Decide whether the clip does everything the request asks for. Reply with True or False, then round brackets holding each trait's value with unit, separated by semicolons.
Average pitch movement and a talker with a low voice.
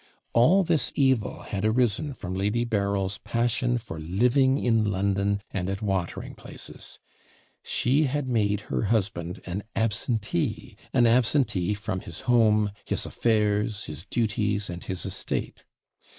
True (3.5 semitones; 105 Hz)